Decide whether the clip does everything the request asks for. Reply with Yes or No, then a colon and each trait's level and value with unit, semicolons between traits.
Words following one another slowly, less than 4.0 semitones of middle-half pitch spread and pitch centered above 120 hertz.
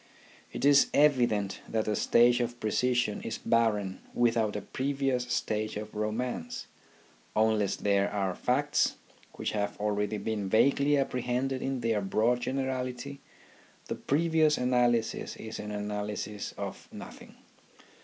No: slow, 125 wpm; average, 3.4 semitones; low, 115 Hz